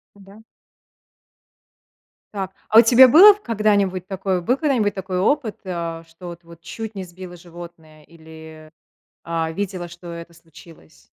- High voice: No, medium, 180 Hz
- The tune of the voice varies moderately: Yes, average, 3.5 semitones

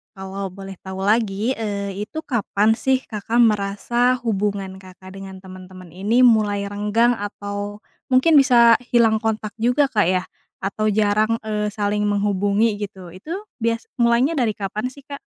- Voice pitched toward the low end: No, high, 210 Hz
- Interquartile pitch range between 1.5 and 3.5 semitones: Yes, average, 2.8 semitones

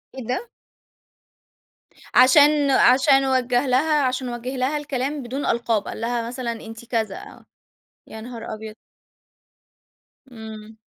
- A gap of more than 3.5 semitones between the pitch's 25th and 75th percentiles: No, average, 2.8 semitones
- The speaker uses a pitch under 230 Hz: No, very high, 250 Hz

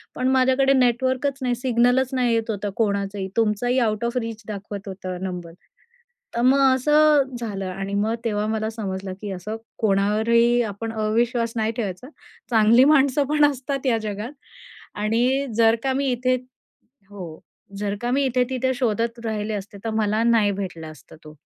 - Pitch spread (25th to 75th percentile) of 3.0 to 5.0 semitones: Yes, average, 3.7 semitones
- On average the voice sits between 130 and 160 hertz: No, high, 230 Hz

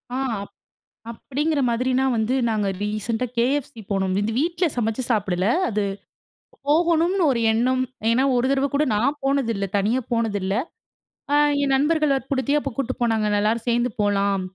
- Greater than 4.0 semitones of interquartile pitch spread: Yes, average, 4.5 semitones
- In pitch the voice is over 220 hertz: Yes, high, 240 Hz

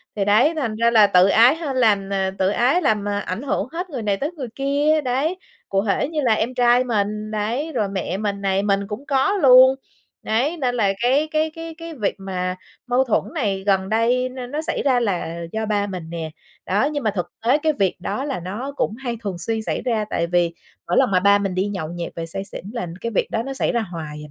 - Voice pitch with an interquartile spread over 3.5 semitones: Yes, average, 5.2 semitones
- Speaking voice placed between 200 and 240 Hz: Yes, high, 220 Hz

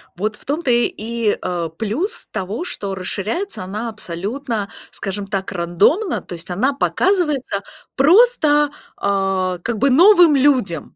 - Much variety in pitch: Yes, wide, 7.2 semitones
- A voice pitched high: Yes, high, 220 Hz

